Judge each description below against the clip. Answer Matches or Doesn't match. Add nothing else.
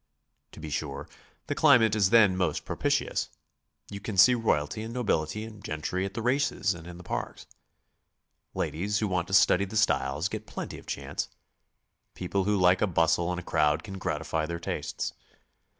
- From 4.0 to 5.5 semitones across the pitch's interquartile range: Matches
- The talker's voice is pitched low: Matches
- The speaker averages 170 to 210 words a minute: Matches